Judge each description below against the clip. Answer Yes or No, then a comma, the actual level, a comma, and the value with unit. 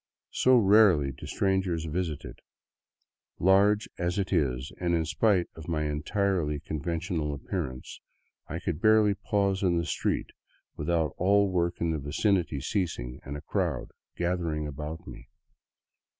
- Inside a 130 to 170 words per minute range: Yes, average, 150 wpm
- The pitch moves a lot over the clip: No, average, 4.2 semitones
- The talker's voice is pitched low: Yes, very low, 85 Hz